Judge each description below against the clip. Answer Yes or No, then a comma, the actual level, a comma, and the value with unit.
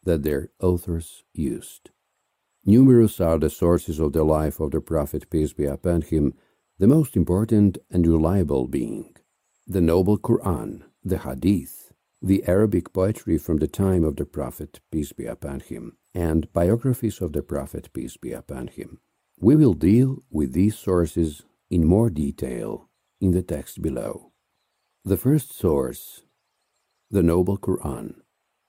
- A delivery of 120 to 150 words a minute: Yes, average, 145 wpm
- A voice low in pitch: Yes, very low, 85 Hz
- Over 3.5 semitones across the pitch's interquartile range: Yes, average, 4.0 semitones